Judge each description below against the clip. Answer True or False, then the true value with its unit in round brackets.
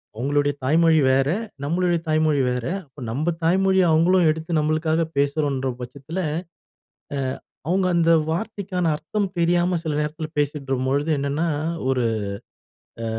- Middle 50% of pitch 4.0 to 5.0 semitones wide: False (3.4 semitones)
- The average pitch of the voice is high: False (155 Hz)